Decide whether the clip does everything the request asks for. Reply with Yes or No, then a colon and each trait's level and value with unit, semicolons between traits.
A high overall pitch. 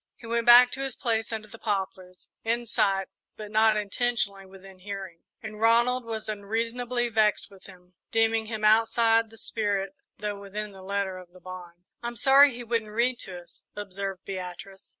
Yes: high, 215 Hz